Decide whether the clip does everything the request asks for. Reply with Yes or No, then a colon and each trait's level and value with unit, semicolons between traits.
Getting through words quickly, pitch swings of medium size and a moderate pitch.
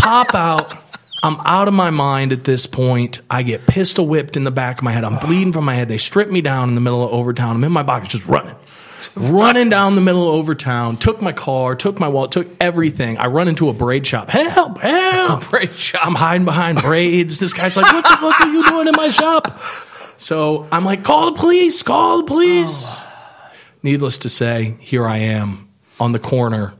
No: fast, 215 wpm; wide, 7.9 semitones; medium, 155 Hz